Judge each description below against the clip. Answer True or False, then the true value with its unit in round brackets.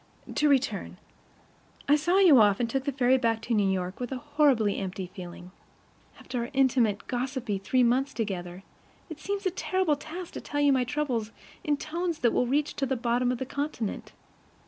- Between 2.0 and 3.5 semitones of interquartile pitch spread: False (4.6 semitones)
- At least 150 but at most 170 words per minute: False (190 wpm)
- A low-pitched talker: False (255 Hz)